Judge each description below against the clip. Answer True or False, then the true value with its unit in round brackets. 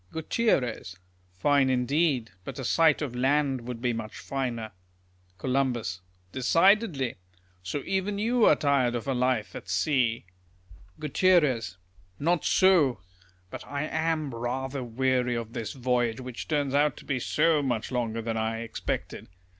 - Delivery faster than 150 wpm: False (140 wpm)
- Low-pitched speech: True (130 Hz)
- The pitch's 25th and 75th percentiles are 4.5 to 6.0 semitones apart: False (4.0 semitones)